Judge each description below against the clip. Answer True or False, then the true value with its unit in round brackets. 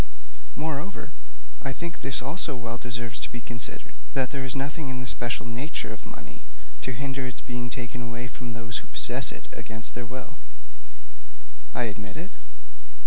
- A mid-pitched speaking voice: False (125 Hz)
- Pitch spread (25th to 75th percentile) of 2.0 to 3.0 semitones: True (2.4 semitones)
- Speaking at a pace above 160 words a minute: True (170 wpm)